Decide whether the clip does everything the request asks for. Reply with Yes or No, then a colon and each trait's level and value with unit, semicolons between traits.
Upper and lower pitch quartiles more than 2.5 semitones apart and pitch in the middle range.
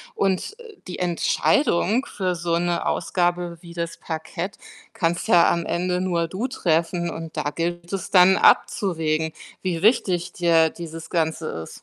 No: narrow, 1.8 semitones; medium, 175 Hz